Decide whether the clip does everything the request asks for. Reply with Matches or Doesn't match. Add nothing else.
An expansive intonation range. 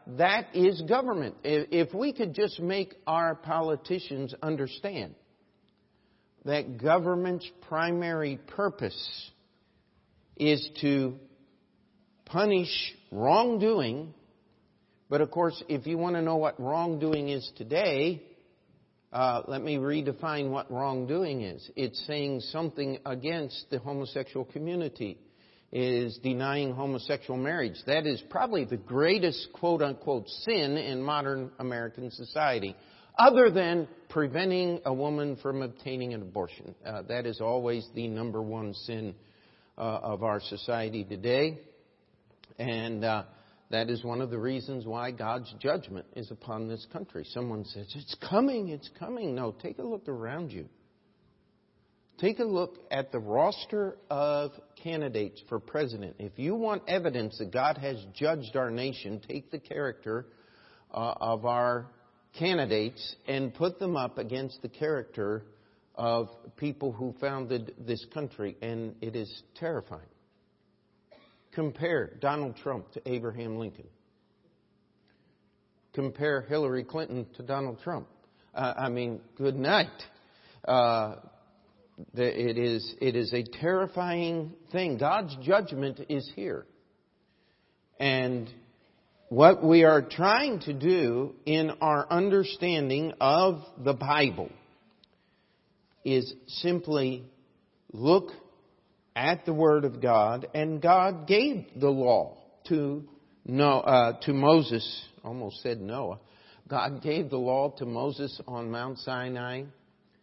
Doesn't match